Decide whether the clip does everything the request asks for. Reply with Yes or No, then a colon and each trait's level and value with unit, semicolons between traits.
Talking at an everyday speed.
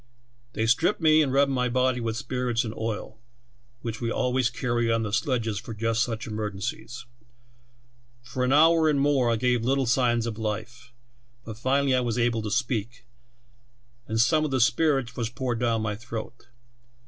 Yes: average, 175 wpm